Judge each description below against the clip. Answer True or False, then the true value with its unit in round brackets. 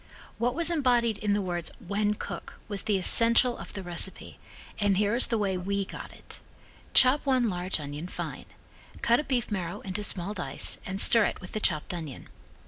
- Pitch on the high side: True (205 Hz)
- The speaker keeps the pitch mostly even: False (4.2 semitones)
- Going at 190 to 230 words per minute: True (195 wpm)